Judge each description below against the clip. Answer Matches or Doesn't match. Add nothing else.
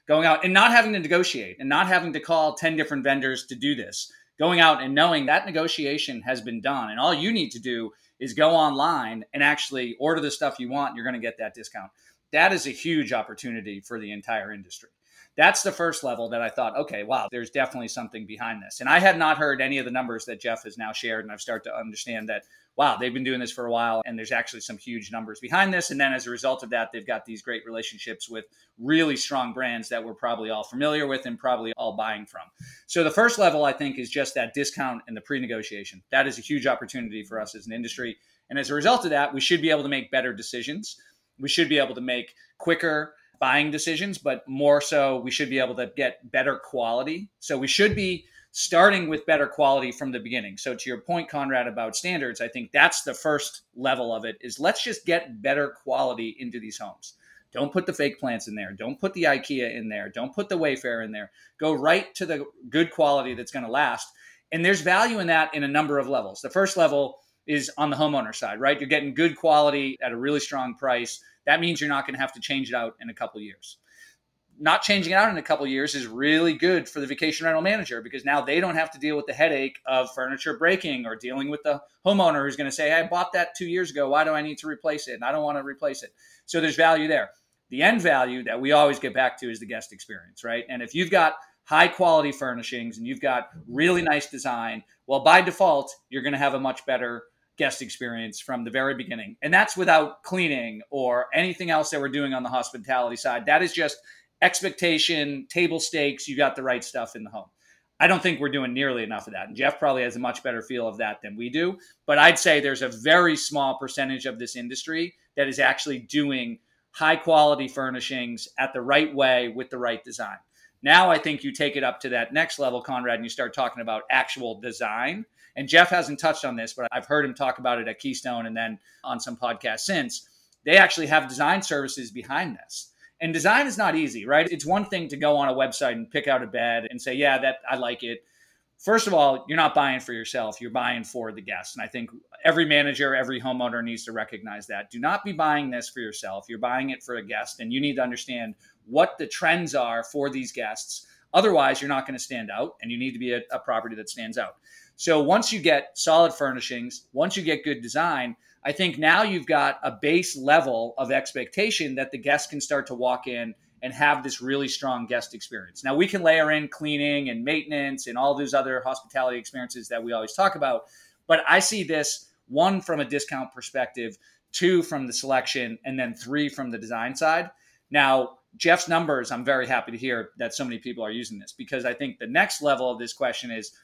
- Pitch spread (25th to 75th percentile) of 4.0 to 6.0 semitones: Matches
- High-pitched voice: Doesn't match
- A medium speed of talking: Doesn't match